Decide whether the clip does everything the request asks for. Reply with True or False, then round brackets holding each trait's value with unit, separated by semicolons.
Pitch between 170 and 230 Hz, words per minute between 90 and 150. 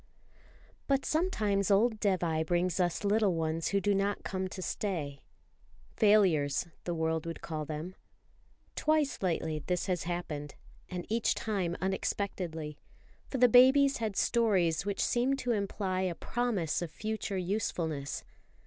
True (185 Hz; 140 wpm)